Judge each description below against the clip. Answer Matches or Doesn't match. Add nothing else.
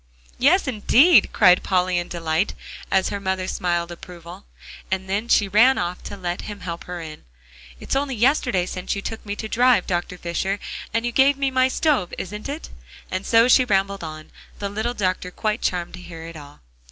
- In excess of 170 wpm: Matches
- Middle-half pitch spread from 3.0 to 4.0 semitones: Doesn't match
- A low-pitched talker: Doesn't match